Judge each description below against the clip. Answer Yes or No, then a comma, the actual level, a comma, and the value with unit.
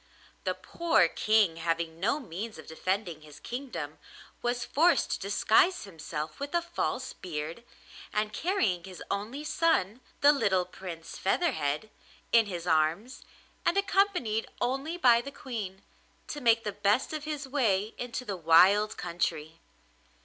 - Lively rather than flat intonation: Yes, wide, 7.3 semitones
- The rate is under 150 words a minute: Yes, average, 140 wpm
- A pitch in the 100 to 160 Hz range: No, high, 210 Hz